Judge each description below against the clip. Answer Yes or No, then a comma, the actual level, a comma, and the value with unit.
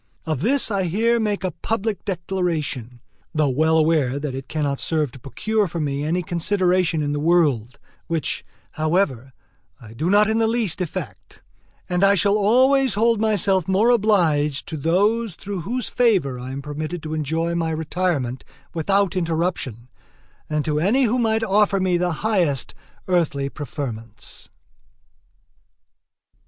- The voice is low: No, medium, 170 Hz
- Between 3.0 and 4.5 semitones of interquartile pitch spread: No, wide, 5.5 semitones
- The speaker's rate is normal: Yes, average, 150 wpm